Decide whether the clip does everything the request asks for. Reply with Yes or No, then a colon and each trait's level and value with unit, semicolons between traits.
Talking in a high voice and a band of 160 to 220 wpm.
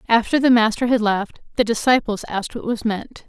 Yes: high, 225 Hz; average, 200 wpm